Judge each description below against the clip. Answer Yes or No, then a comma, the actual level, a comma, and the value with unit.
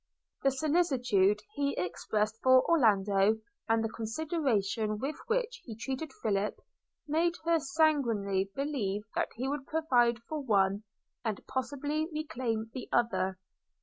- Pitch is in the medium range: No, high, 245 Hz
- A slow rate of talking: Yes, slow, 125 wpm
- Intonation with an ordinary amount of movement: No, wide, 5.9 semitones